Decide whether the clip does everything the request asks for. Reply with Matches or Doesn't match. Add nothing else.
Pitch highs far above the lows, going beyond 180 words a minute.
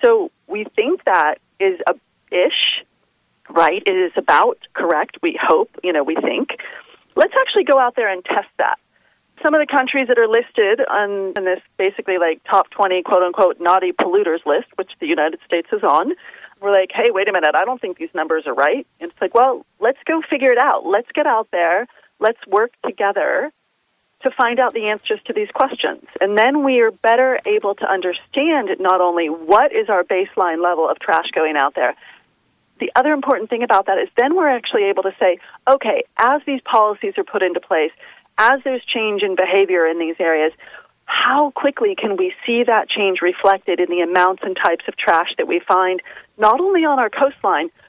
Matches